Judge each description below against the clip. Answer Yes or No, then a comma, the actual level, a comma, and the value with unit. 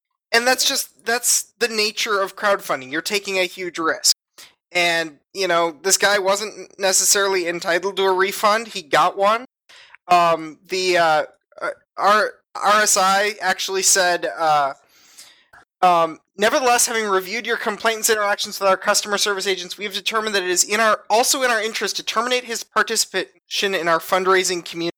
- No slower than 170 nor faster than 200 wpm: No, average, 160 wpm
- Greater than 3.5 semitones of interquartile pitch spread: No, average, 3.1 semitones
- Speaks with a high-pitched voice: Yes, high, 195 Hz